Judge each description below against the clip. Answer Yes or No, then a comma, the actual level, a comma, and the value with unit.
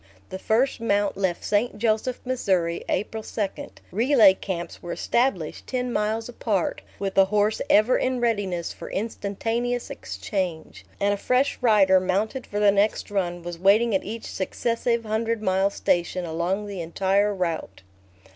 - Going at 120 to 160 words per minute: Yes, average, 150 wpm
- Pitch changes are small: No, average, 3.3 semitones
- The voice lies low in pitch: No, high, 205 Hz